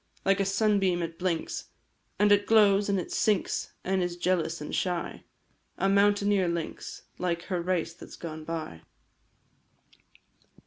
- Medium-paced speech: Yes, average, 145 wpm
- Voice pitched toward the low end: No, medium, 185 Hz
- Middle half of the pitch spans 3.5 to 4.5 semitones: No, average, 2.9 semitones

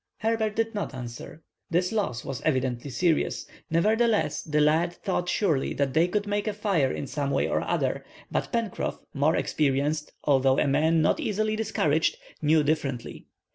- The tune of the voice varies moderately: No, wide, 6.5 semitones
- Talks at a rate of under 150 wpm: No, average, 160 wpm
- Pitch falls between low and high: Yes, medium, 160 Hz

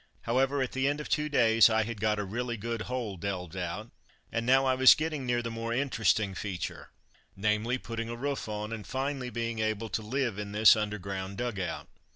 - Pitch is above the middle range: No, low, 115 Hz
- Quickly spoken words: Yes, fast, 210 wpm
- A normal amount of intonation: Yes, average, 3.3 semitones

